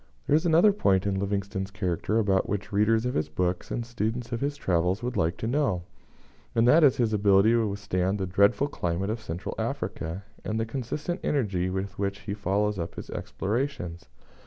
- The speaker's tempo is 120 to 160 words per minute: No, average, 190 wpm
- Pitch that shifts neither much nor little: Yes, average, 3.8 semitones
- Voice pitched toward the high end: No, low, 100 Hz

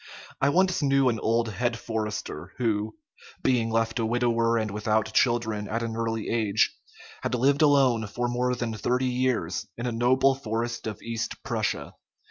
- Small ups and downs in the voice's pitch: Yes, narrow, 2.1 semitones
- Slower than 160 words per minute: No, average, 165 wpm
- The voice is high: No, low, 115 Hz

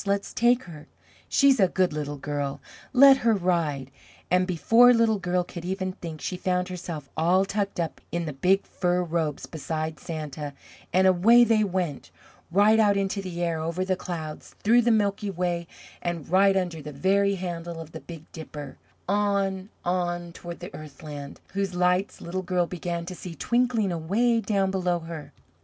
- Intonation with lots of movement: No, average, 3.2 semitones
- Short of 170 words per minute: No, average, 175 wpm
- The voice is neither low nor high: Yes, medium, 180 Hz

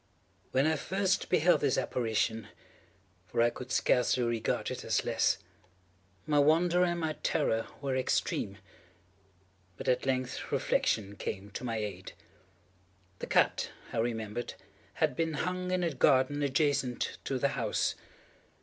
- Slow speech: Yes, slow, 130 wpm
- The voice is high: No, low, 130 Hz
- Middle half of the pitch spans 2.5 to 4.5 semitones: No, wide, 5.5 semitones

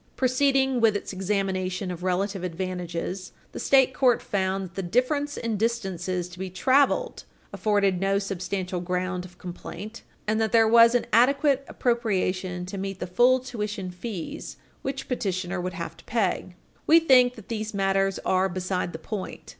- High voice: Yes, high, 195 Hz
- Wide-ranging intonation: No, average, 4.3 semitones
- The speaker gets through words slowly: No, average, 160 wpm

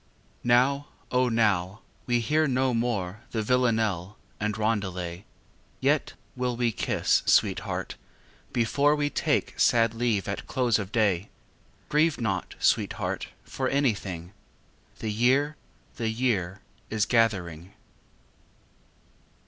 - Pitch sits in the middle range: No, low, 115 Hz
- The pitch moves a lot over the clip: No, average, 3.9 semitones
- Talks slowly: Yes, slow, 110 wpm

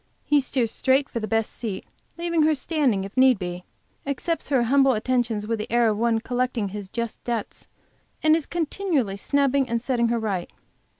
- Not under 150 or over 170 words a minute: No, average, 185 wpm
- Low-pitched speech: No, high, 240 Hz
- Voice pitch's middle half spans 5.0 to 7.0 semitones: No, average, 4.2 semitones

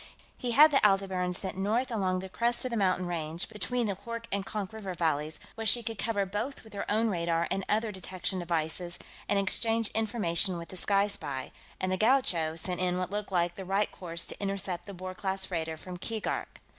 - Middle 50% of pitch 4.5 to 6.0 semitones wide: No, average, 3.5 semitones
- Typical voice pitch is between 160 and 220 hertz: Yes, high, 190 Hz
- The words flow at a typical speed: No, fast, 210 wpm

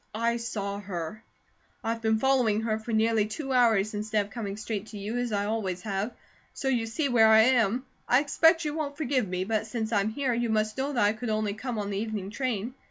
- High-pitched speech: Yes, high, 220 Hz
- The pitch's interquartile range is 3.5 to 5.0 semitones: No, average, 2.8 semitones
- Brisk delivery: Yes, fast, 230 wpm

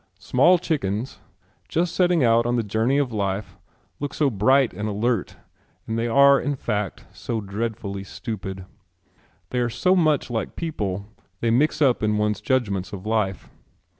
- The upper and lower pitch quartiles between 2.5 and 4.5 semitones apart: No, average, 5.0 semitones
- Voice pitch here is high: No, low, 115 Hz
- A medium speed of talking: Yes, average, 165 wpm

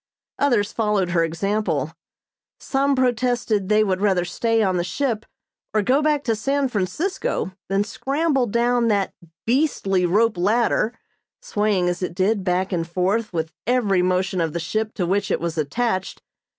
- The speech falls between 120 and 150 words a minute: No, average, 160 wpm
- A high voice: Yes, high, 210 Hz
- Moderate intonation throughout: Yes, average, 4.7 semitones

